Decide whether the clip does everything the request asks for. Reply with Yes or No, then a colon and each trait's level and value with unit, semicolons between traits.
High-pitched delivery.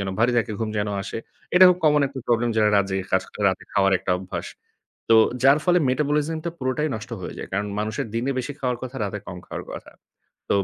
No: low, 120 Hz